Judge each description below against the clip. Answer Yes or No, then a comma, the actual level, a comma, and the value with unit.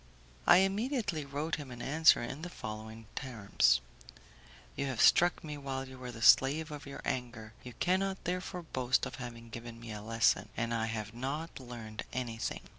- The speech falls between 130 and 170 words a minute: No, average, 180 wpm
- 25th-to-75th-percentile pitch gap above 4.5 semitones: Yes, average, 5.2 semitones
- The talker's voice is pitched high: No, low, 130 Hz